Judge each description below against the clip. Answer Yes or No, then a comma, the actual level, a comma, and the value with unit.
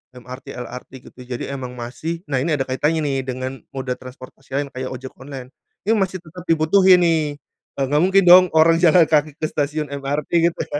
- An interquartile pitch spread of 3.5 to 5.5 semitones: Yes, average, 4.1 semitones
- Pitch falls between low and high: Yes, medium, 145 Hz